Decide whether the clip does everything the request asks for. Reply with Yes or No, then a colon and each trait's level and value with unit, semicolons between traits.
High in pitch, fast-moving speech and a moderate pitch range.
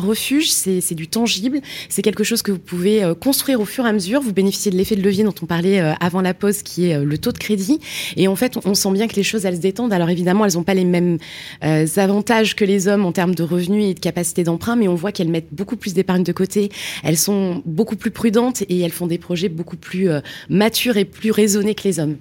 Yes: high, 195 Hz; fast, 275 wpm; average, 3.4 semitones